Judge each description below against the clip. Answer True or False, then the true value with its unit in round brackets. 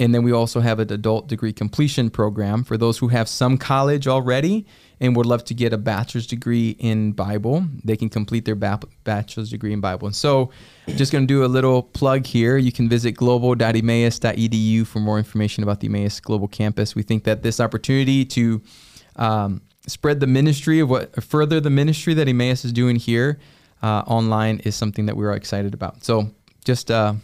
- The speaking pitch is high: False (115 Hz)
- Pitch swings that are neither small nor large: True (3.1 semitones)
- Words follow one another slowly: False (195 wpm)